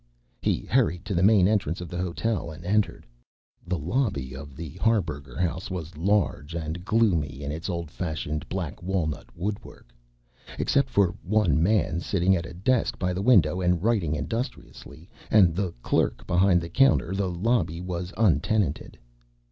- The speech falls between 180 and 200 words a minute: No, average, 160 wpm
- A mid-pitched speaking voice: No, very low, 90 Hz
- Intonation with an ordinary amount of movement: Yes, average, 3.8 semitones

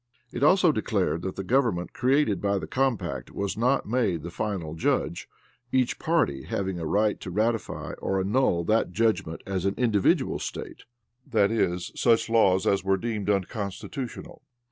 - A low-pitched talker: Yes, low, 105 Hz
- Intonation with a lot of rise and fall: No, average, 4.0 semitones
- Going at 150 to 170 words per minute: Yes, average, 160 wpm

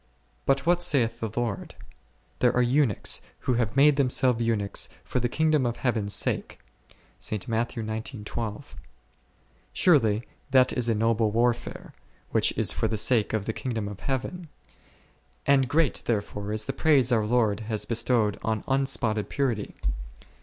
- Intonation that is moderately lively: Yes, average, 3.5 semitones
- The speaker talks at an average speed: Yes, average, 155 wpm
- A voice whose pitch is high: No, low, 120 Hz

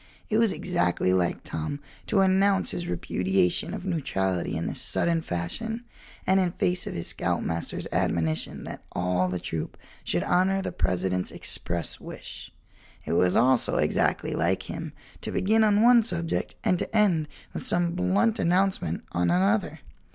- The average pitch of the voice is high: No, medium, 160 Hz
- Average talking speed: Yes, average, 155 wpm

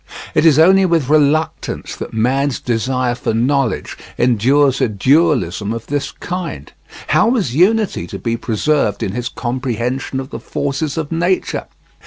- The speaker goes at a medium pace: Yes, average, 150 wpm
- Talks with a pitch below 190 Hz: Yes, low, 135 Hz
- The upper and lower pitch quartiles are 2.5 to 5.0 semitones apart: Yes, average, 4.7 semitones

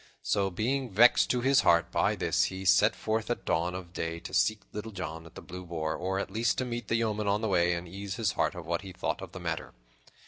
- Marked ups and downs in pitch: No, average, 4.1 semitones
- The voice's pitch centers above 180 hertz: No, very low, 95 Hz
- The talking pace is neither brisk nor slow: No, fast, 255 wpm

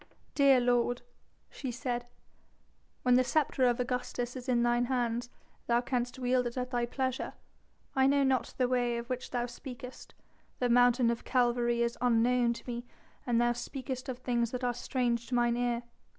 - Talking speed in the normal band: Yes, average, 180 wpm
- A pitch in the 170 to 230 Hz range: No, high, 245 Hz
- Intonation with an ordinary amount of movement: No, narrow, 1.0 semitones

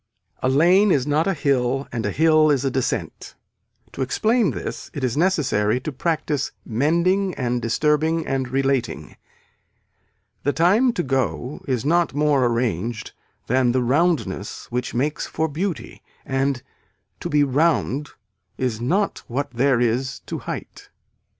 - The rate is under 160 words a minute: Yes, average, 145 wpm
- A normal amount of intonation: Yes, average, 4.3 semitones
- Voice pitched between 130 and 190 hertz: Yes, medium, 140 Hz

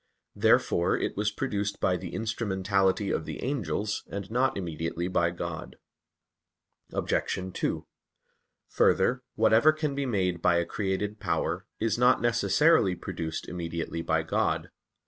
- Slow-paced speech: Yes, slow, 130 wpm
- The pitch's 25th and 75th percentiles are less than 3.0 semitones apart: No, average, 4.6 semitones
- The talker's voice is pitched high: No, low, 100 Hz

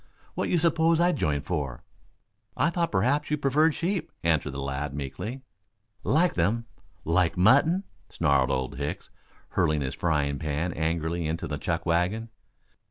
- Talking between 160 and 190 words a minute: No, average, 150 wpm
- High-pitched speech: No, very low, 85 Hz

